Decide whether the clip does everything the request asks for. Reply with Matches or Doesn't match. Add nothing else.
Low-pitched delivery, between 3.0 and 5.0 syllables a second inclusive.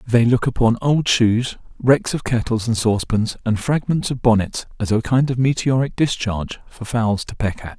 Matches